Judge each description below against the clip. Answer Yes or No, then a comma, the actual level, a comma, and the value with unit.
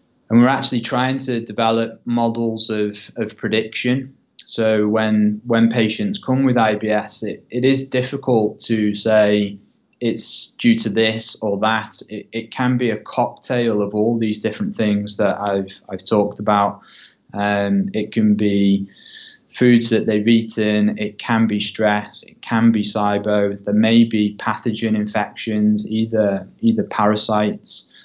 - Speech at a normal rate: Yes, average, 150 wpm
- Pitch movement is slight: Yes, narrow, 1.8 semitones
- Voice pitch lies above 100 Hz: Yes, low, 110 Hz